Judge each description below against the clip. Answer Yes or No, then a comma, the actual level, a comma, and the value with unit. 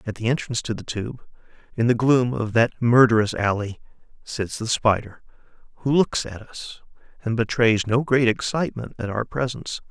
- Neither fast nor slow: Yes, average, 170 wpm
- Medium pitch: No, low, 115 Hz